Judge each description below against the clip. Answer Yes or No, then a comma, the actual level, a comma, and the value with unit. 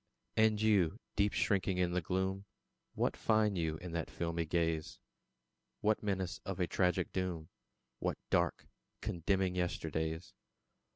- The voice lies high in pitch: No, very low, 90 Hz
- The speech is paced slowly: Yes, slow, 130 wpm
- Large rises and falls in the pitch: No, average, 2.8 semitones